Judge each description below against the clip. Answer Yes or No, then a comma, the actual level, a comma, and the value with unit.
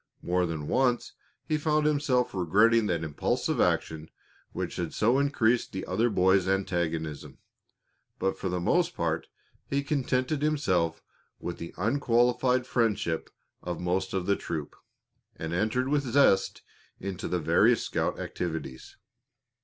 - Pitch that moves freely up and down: Yes, wide, 6.5 semitones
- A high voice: No, low, 100 Hz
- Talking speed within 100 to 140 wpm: Yes, slow, 135 wpm